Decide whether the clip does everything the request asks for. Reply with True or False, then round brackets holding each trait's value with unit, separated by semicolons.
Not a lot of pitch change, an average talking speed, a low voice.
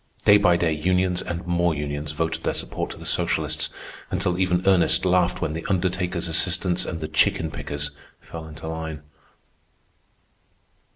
True (2.3 semitones; 155 wpm; 85 Hz)